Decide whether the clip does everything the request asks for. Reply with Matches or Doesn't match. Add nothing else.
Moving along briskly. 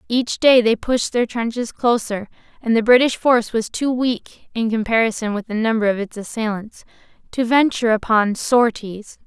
Doesn't match